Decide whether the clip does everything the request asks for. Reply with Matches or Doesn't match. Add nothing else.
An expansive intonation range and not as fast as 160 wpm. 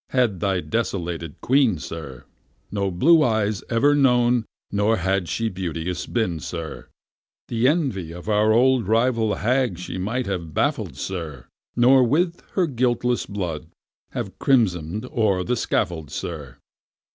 Matches